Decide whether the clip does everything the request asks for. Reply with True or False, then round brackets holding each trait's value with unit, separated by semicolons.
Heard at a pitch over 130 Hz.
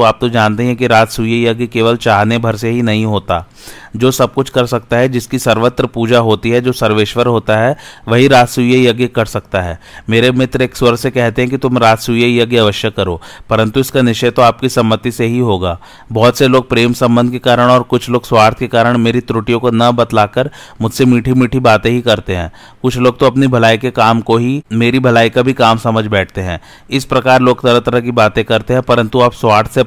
False (120 Hz)